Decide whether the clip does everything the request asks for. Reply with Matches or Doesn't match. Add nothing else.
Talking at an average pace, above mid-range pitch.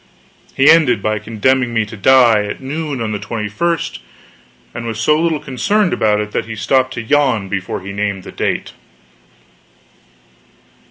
Doesn't match